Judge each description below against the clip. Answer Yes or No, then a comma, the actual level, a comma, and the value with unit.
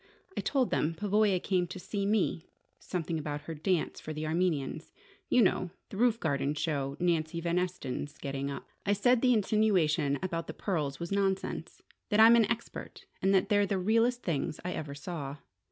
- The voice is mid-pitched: Yes, medium, 180 Hz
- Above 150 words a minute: Yes, average, 185 wpm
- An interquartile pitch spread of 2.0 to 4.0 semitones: No, average, 4.9 semitones